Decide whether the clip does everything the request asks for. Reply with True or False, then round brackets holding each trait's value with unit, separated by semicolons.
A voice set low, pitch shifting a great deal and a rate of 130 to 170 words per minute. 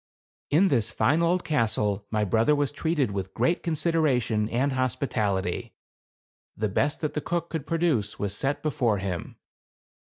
True (130 Hz; 6.7 semitones; 150 wpm)